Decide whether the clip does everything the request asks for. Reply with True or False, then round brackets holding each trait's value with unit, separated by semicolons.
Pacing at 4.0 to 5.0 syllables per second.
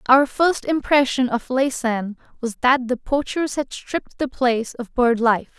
True (4.3 syllables/s)